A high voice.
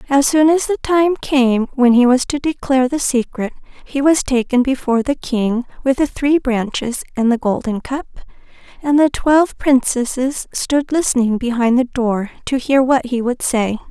Yes: very high, 260 Hz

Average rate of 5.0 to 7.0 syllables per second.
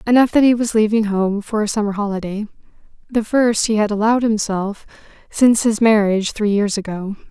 Yes: 5.7 syllables/s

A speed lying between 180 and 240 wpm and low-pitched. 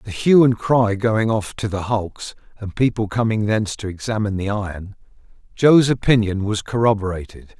No: average, 165 wpm; low, 110 Hz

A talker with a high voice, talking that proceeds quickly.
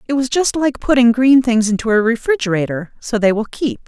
Yes: high, 240 Hz; fast, 215 wpm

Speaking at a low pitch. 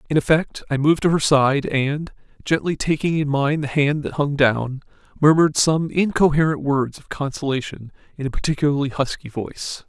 No: medium, 145 Hz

